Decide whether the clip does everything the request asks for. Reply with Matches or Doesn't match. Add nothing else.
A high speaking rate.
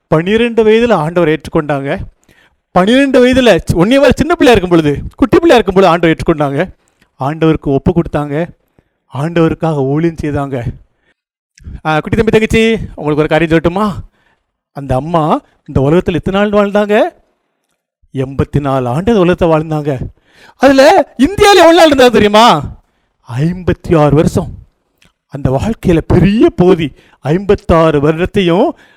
Doesn't match